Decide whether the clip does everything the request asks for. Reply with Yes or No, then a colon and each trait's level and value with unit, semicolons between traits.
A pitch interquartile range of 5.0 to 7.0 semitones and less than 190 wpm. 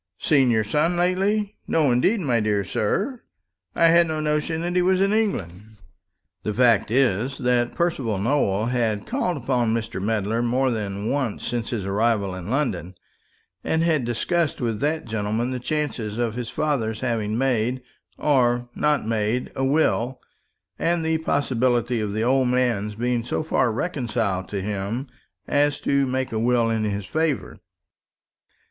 Yes: average, 5.3 semitones; average, 160 wpm